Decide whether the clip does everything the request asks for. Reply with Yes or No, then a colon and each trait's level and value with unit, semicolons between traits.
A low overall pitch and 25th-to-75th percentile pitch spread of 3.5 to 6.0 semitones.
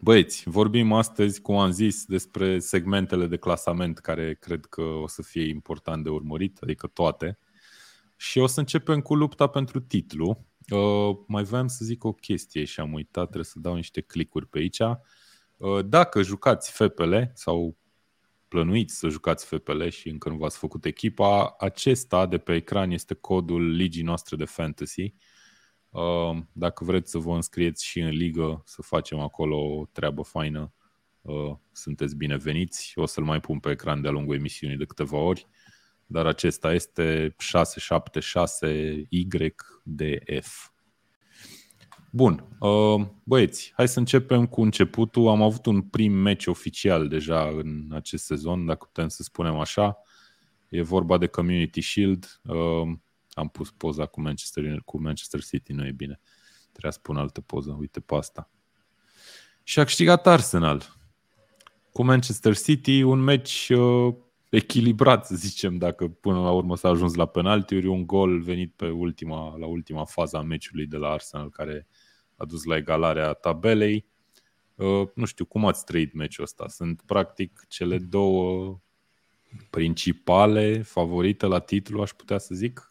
Yes: very low, 90 Hz; average, 4.7 semitones